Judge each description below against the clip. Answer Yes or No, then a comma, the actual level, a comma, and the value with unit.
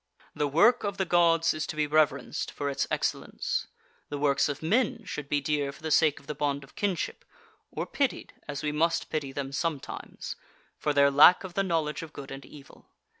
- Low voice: No, medium, 150 Hz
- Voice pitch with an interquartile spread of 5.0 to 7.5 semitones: No, average, 2.7 semitones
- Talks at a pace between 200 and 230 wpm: Yes, fast, 205 wpm